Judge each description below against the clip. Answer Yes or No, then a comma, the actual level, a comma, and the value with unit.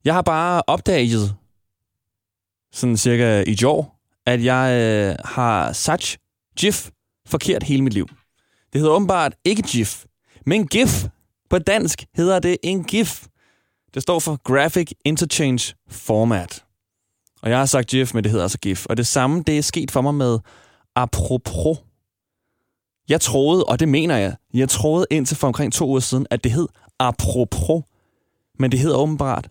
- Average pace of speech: Yes, average, 160 wpm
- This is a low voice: Yes, low, 125 Hz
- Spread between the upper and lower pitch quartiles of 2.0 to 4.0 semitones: No, wide, 5.6 semitones